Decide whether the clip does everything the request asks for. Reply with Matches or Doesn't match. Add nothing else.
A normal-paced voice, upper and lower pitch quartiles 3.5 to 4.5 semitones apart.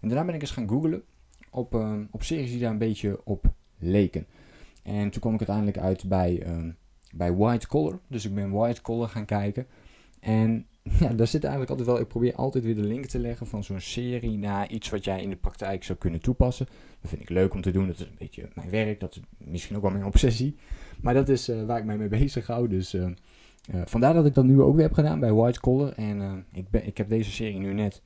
Doesn't match